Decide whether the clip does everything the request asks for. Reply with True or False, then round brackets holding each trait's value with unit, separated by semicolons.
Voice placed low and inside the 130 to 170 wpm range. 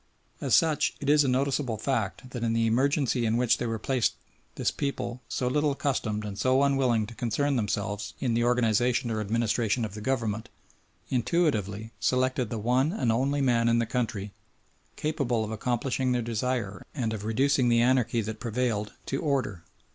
False (120 Hz; 180 wpm)